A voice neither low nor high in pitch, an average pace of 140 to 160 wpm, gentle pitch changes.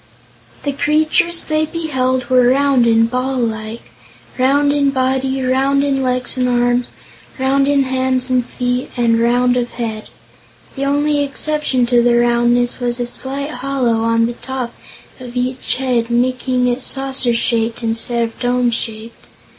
No: very high, 255 Hz; average, 155 wpm; narrow, 2.1 semitones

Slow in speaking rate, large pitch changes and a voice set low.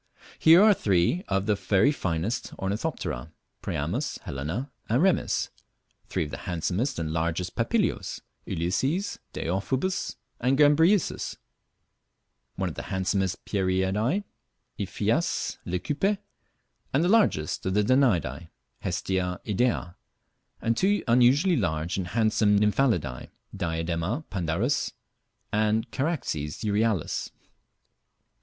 Yes: slow, 105 wpm; wide, 7.5 semitones; low, 105 Hz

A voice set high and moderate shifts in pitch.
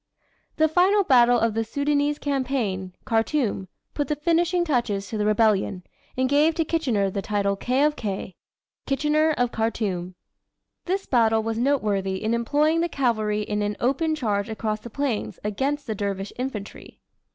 No: high, 235 Hz; wide, 5.7 semitones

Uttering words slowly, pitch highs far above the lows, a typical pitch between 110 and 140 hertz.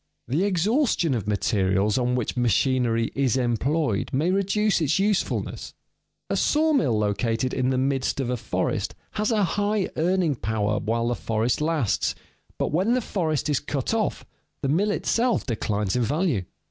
No: average, 160 wpm; wide, 8.6 semitones; low, 135 Hz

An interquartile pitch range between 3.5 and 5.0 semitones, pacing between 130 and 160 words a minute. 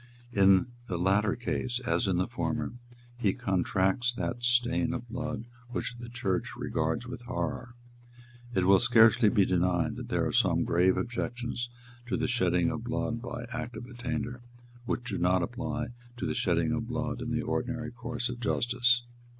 No: average, 4.0 semitones; average, 175 wpm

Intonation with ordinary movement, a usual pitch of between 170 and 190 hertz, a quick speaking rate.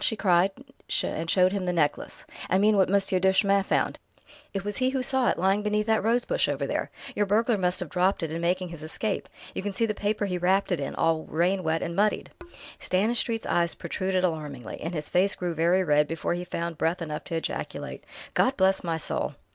Yes: average, 3.4 semitones; medium, 185 Hz; fast, 220 wpm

